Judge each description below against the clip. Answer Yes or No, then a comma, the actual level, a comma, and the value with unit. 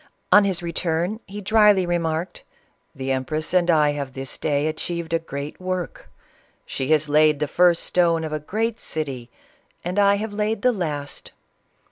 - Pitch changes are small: No, average, 3.8 semitones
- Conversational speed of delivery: Yes, average, 175 wpm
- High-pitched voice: No, medium, 165 Hz